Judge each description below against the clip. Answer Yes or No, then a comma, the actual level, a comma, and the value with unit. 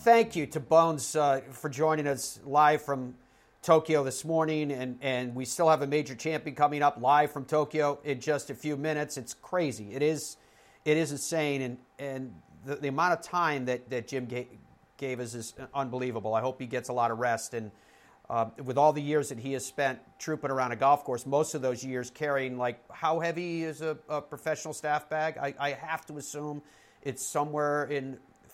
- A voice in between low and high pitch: Yes, medium, 145 Hz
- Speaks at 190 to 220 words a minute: Yes, fast, 205 wpm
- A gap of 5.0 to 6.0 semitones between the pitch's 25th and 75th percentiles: No, average, 2.9 semitones